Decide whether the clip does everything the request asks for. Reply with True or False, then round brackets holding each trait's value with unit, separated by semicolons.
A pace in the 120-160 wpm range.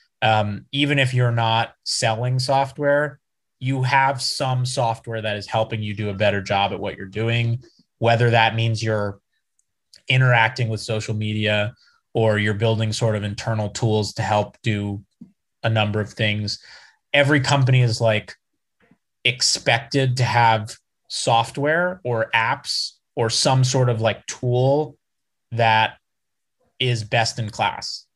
True (140 wpm)